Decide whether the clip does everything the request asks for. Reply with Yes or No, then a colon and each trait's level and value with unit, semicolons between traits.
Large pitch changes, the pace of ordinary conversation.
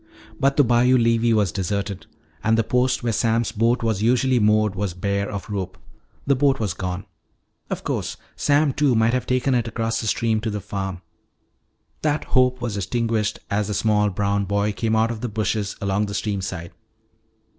No: average, 3.0 semitones; average, 190 wpm